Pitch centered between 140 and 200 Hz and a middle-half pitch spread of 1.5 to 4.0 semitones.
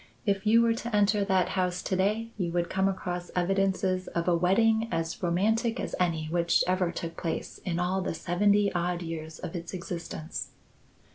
Yes: medium, 185 Hz; average, 2.8 semitones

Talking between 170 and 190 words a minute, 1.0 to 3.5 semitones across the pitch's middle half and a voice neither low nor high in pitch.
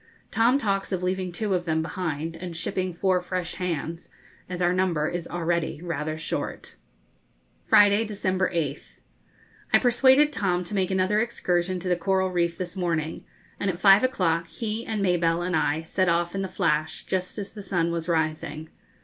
Yes: average, 175 wpm; narrow, 2.6 semitones; medium, 180 Hz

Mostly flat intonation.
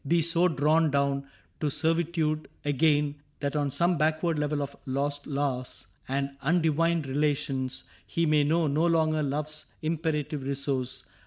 Yes: narrow, 2.3 semitones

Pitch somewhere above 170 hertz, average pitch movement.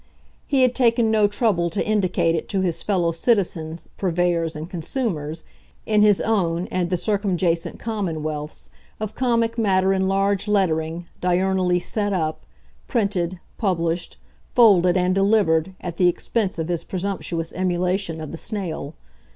Yes: medium, 185 Hz; average, 3.5 semitones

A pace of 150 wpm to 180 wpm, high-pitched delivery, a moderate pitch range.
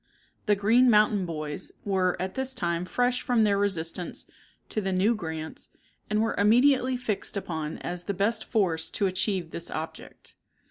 Yes: average, 165 wpm; high, 200 Hz; average, 4.4 semitones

